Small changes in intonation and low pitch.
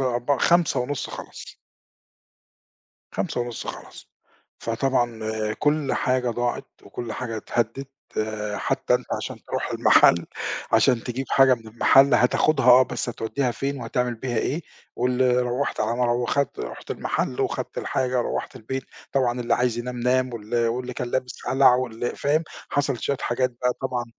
Yes: narrow, 1.8 semitones; low, 125 Hz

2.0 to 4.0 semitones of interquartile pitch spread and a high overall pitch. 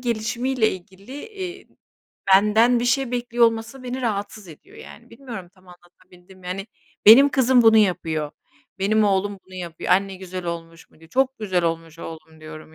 No: average, 5.3 semitones; high, 200 Hz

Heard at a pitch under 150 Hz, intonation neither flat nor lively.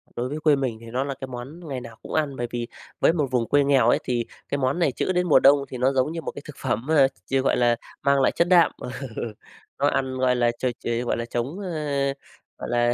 Yes: low, 135 Hz; average, 3.4 semitones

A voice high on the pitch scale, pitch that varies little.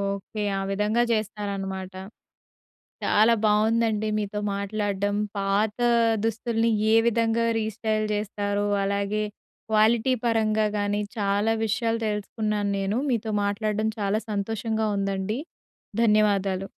Yes: high, 210 Hz; narrow, 1.6 semitones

